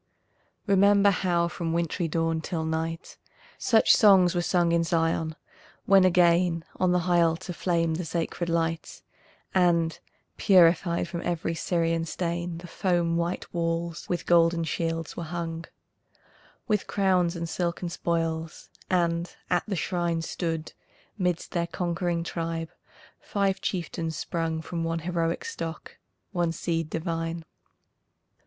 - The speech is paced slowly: Yes, slow, 130 wpm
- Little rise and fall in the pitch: Yes, narrow, 1.3 semitones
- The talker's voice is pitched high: No, medium, 170 Hz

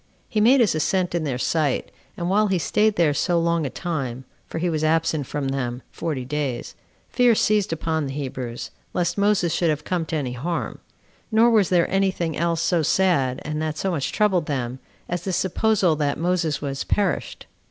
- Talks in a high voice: No, medium, 165 Hz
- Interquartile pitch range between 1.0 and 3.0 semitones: No, average, 4.3 semitones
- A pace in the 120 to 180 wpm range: No, average, 195 wpm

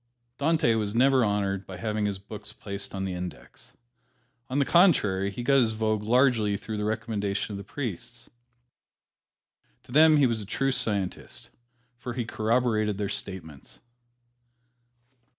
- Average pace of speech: Yes, average, 150 wpm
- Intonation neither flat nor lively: Yes, average, 3.7 semitones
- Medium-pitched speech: No, low, 110 Hz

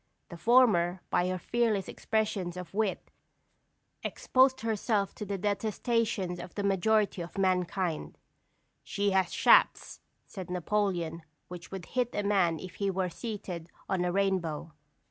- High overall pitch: Yes, high, 195 Hz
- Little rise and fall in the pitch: No, average, 3.0 semitones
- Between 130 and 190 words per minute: Yes, average, 140 wpm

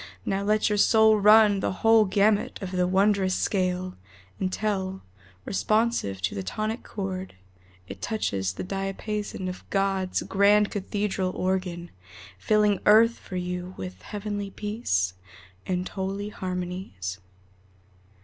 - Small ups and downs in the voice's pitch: Yes, narrow, 2.3 semitones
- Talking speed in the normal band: No, slow, 120 wpm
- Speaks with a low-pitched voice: No, high, 195 Hz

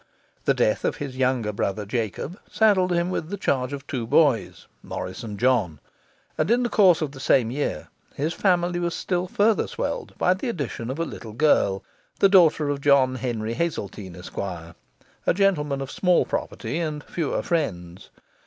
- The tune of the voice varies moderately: No, wide, 7.2 semitones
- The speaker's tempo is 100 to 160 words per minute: No, average, 175 wpm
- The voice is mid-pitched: Yes, medium, 145 Hz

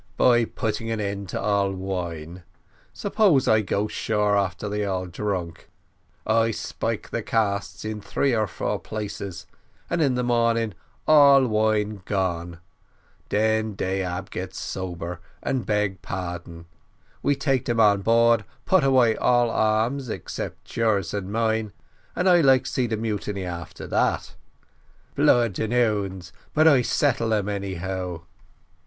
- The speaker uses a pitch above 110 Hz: No, low, 105 Hz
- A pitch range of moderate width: Yes, average, 3.5 semitones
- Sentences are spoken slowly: No, average, 145 wpm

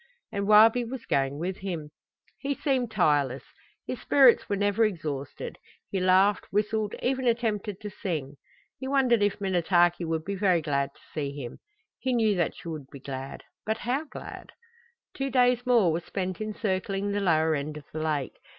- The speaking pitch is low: No, high, 195 Hz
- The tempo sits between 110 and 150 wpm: No, average, 180 wpm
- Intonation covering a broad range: Yes, wide, 6.0 semitones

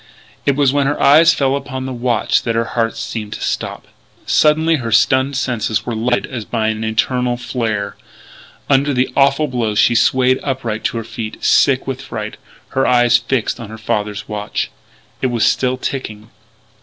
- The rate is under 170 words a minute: No, average, 180 wpm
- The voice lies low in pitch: Yes, low, 120 Hz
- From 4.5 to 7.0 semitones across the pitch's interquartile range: No, average, 3.1 semitones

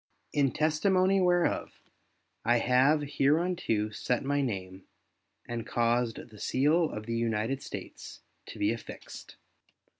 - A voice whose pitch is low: Yes, low, 130 Hz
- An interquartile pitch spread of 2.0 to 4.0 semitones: No, average, 5.2 semitones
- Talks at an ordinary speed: No, slow, 120 wpm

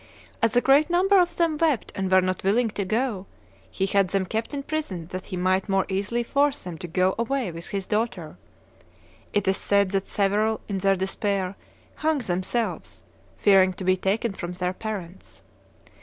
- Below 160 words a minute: No, average, 185 wpm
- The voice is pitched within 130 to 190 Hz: No, high, 200 Hz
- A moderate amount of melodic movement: Yes, average, 4.1 semitones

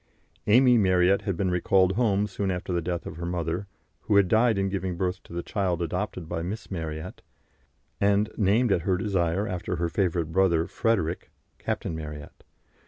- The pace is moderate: Yes, average, 175 wpm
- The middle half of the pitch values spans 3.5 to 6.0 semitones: No, average, 2.8 semitones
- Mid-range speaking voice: No, very low, 95 Hz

